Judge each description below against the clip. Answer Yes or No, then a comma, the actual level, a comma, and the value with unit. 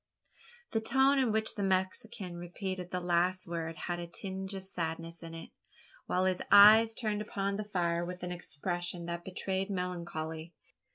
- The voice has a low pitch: No, medium, 180 Hz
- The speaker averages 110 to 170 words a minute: Yes, average, 165 wpm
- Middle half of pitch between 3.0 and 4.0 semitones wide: No, narrow, 2.6 semitones